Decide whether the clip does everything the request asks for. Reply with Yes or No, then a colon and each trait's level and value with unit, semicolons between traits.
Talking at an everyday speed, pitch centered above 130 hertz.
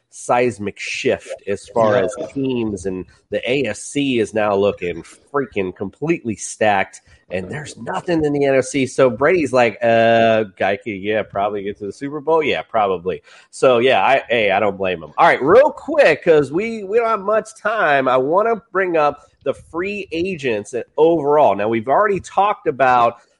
Yes: average, 175 wpm; medium, 140 Hz